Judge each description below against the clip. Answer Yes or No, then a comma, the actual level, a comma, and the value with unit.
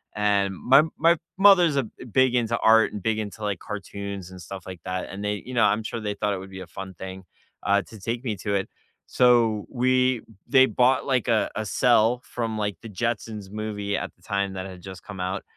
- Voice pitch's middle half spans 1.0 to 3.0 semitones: No, average, 3.6 semitones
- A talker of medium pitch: No, low, 105 Hz